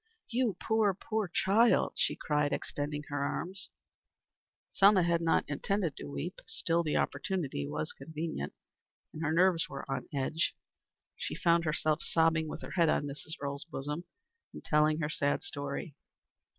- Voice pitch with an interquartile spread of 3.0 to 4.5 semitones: Yes, average, 3.4 semitones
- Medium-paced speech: Yes, average, 150 wpm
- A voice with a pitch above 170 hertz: No, medium, 155 Hz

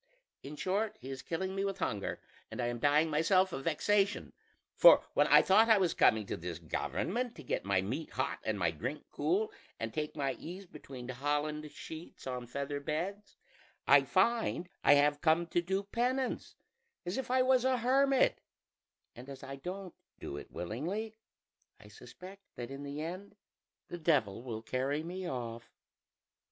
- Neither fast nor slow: Yes, average, 175 wpm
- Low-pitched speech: No, medium, 155 Hz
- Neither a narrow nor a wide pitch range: No, wide, 6.8 semitones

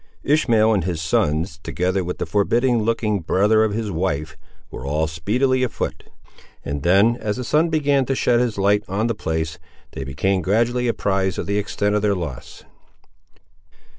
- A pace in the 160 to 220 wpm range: Yes, average, 170 wpm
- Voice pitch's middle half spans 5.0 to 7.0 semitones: Yes, wide, 5.5 semitones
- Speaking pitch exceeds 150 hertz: No, low, 100 Hz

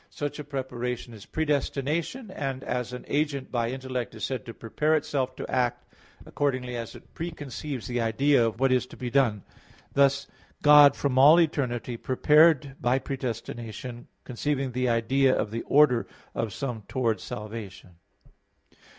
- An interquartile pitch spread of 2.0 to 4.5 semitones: Yes, average, 3.0 semitones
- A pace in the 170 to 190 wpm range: No, average, 150 wpm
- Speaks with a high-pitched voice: No, low, 130 Hz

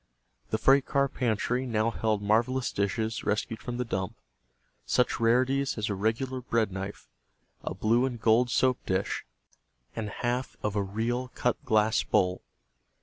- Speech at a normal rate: Yes, average, 150 wpm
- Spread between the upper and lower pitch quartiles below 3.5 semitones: Yes, average, 2.9 semitones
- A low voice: Yes, low, 115 Hz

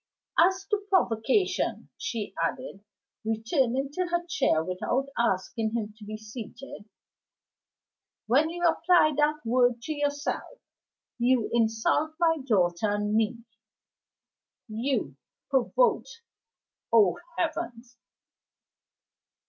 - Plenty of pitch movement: Yes, wide, 6.0 semitones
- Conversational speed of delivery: No, slow, 100 wpm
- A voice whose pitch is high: Yes, high, 245 Hz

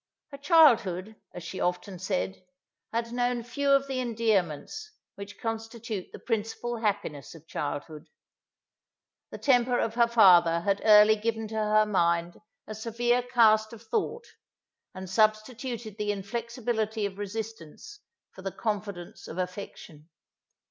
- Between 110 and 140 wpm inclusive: Yes, slow, 135 wpm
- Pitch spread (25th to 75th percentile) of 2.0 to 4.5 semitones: Yes, average, 3.9 semitones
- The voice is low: No, high, 215 Hz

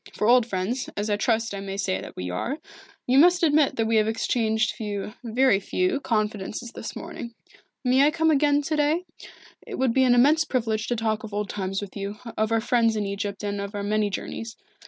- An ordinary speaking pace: No, fast, 220 wpm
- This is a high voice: Yes, high, 225 Hz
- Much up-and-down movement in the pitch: No, average, 4.1 semitones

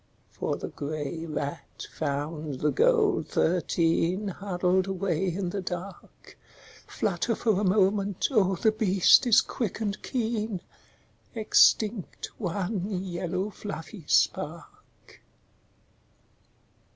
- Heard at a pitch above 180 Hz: Yes, high, 190 Hz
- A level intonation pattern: No, average, 3.5 semitones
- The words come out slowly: Yes, slow, 105 wpm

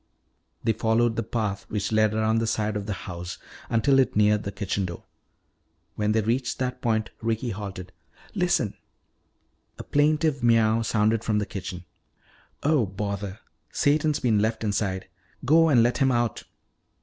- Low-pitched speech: Yes, low, 110 Hz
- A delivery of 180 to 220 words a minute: No, average, 155 wpm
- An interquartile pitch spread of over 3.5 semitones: No, average, 2.7 semitones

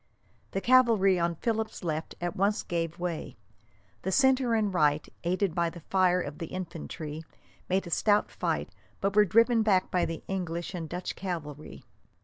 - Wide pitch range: No, average, 3.6 semitones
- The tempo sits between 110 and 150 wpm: No, average, 165 wpm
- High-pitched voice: No, medium, 180 Hz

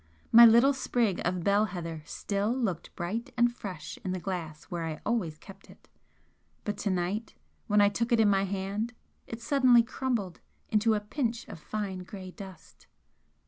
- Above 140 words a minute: Yes, average, 175 wpm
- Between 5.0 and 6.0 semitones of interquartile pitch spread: No, average, 4.0 semitones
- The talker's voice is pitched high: Yes, high, 205 Hz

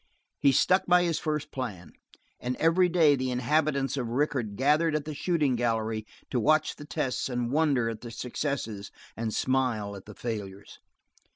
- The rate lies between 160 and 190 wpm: Yes, average, 170 wpm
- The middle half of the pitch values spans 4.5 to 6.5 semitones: Yes, average, 5.0 semitones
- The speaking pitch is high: No, low, 130 Hz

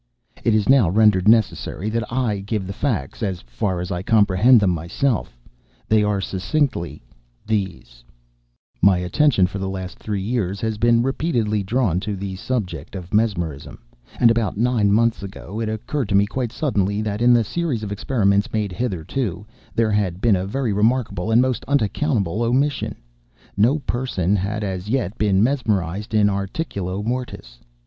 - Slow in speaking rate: No, average, 160 wpm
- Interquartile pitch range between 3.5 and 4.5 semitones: Yes, average, 3.8 semitones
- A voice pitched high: No, low, 105 Hz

